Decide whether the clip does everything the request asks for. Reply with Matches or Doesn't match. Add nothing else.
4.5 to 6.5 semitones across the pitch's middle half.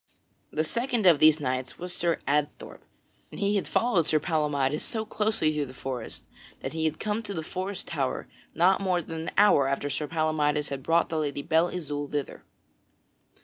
Doesn't match